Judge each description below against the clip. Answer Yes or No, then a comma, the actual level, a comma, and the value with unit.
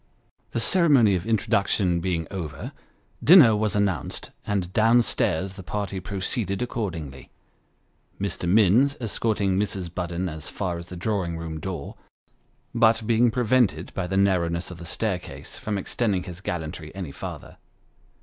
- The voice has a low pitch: Yes, very low, 95 Hz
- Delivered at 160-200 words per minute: No, average, 140 wpm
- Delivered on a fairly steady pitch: No, average, 4.0 semitones